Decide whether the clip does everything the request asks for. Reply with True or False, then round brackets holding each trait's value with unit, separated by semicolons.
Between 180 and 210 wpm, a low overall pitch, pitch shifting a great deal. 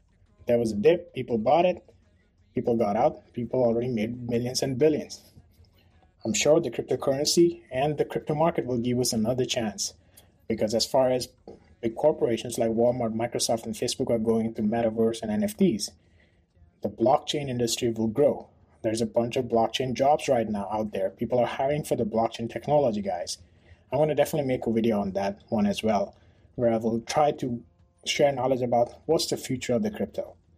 False (185 wpm; 115 Hz; 3.7 semitones)